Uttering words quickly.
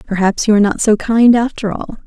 Yes: fast, 230 wpm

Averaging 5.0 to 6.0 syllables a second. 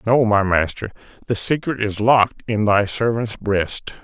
No: 4.4 syllables/s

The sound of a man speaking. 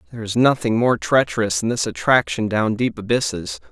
Yes: male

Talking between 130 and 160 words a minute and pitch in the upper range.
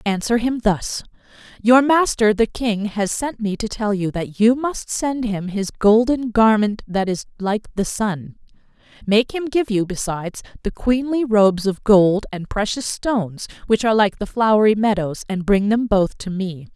No: average, 185 wpm; high, 215 Hz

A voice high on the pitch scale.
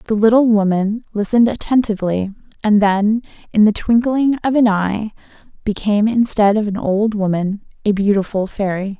Yes: high, 210 Hz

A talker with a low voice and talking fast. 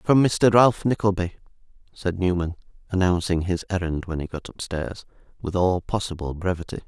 No: very low, 90 Hz; average, 150 wpm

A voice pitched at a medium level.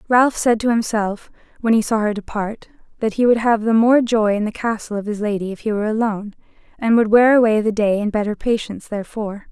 No: high, 220 Hz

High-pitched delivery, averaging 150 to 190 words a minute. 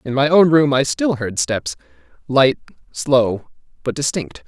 No: low, 135 Hz; average, 160 wpm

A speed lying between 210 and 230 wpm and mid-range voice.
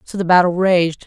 Yes: fast, 225 wpm; medium, 180 Hz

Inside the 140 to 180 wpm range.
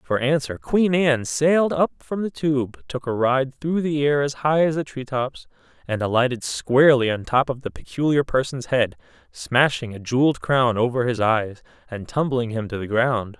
No: average, 195 wpm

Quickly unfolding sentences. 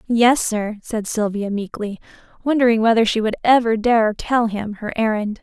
No: average, 165 wpm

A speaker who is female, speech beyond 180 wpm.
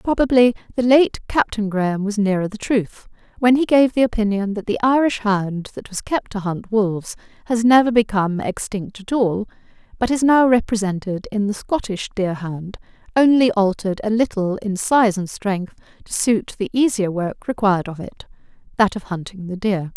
No: female; average, 175 wpm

